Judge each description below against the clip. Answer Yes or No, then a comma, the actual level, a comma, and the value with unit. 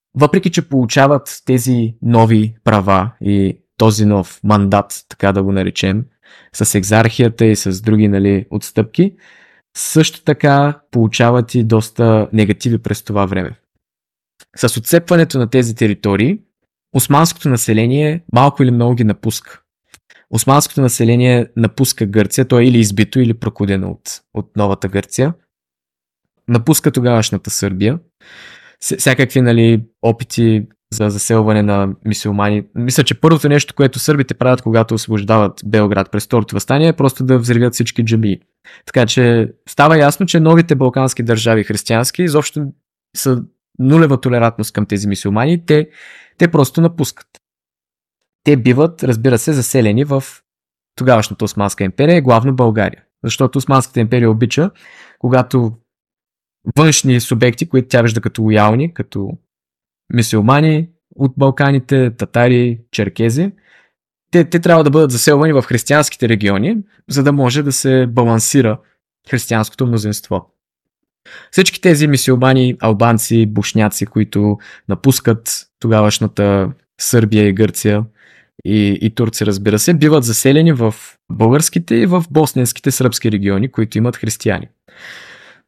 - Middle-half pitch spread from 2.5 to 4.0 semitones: No, average, 4.5 semitones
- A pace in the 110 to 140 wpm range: Yes, average, 125 wpm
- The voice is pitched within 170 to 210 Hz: No, low, 120 Hz